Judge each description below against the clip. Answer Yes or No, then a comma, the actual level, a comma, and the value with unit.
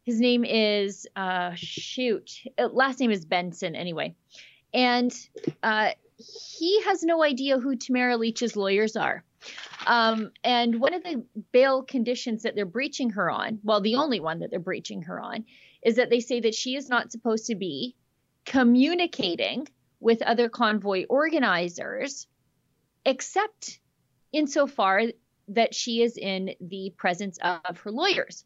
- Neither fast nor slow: Yes, average, 150 wpm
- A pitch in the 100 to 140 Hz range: No, high, 235 Hz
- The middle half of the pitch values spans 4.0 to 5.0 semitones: Yes, average, 4.6 semitones